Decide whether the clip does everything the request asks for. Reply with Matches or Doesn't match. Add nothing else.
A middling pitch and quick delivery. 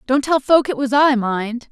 Doesn't match